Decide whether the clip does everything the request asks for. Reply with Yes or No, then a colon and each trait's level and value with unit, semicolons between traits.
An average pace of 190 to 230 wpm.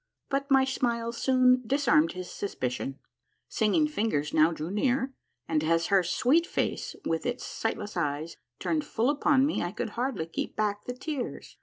No: average, 165 wpm